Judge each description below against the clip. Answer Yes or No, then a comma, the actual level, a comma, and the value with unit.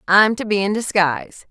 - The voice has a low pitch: No, high, 190 Hz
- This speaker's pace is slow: No, average, 200 wpm